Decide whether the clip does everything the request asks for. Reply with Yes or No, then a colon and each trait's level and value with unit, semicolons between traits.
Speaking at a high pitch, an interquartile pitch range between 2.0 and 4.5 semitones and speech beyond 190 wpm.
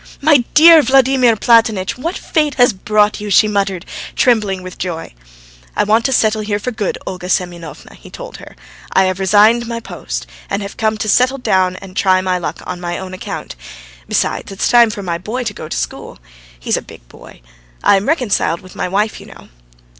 Yes: high, 210 Hz; average, 4.2 semitones; average, 200 wpm